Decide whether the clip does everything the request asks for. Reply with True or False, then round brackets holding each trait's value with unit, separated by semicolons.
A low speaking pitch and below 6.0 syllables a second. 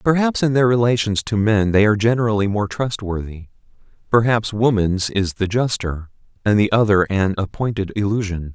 True (105 Hz; 5.3 syllables/s)